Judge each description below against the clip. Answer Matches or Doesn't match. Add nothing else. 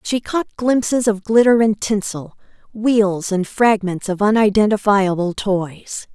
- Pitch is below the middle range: Doesn't match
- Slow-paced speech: Matches